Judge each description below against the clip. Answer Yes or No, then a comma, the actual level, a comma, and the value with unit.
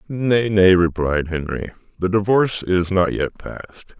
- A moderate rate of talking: Yes, average, 150 wpm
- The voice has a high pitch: No, very low, 95 Hz